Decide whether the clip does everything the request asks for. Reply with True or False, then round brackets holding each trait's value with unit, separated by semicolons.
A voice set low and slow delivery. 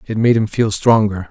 False (105 Hz; 230 wpm)